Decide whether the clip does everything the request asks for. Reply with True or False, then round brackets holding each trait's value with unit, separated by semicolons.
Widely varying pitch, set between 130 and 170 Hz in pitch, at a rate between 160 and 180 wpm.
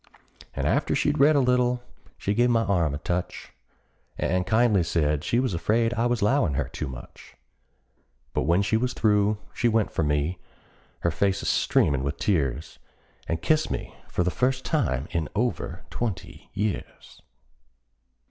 False (6.6 semitones; 100 Hz; 165 wpm)